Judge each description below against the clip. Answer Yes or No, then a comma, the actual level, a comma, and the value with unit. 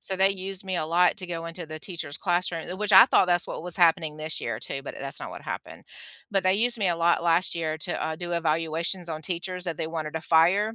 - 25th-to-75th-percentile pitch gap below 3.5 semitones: Yes, narrow, 2.6 semitones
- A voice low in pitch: No, medium, 170 Hz